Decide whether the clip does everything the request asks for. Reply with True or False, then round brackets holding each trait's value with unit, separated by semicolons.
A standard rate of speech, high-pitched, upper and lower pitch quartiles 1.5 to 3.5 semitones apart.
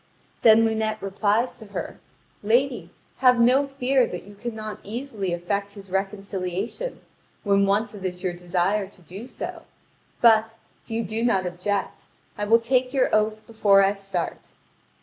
True (155 wpm; 210 Hz; 2.9 semitones)